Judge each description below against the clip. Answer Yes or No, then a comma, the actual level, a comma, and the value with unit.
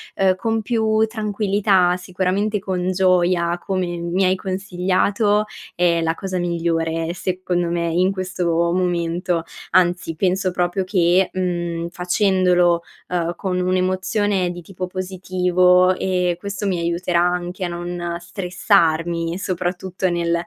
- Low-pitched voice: No, medium, 180 Hz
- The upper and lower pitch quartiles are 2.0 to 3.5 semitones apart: No, narrow, 1.4 semitones